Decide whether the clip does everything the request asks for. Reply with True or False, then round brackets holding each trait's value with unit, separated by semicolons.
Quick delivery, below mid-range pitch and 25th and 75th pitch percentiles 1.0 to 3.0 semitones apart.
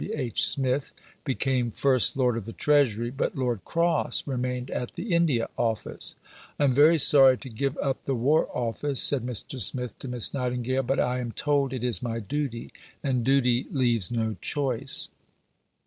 False (175 wpm; 130 Hz; 2.5 semitones)